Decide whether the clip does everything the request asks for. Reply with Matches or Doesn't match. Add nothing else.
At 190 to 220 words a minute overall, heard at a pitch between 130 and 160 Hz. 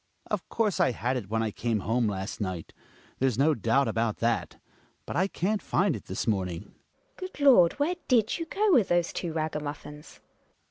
Matches